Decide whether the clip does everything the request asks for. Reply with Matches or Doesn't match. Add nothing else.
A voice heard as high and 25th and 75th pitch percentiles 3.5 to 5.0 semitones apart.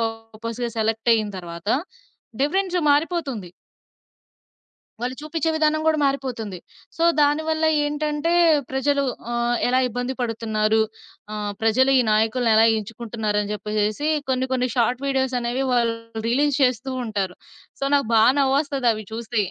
Matches